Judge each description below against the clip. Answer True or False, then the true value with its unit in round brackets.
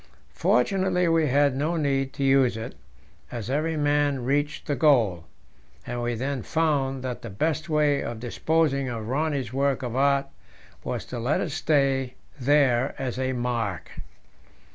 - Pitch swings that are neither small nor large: True (3.0 semitones)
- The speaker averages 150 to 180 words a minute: True (155 wpm)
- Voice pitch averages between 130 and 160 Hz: True (135 Hz)